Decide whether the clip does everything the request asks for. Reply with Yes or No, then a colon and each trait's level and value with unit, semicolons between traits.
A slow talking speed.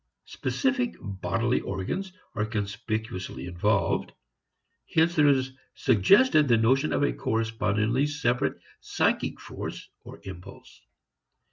Yes: slow, 105 wpm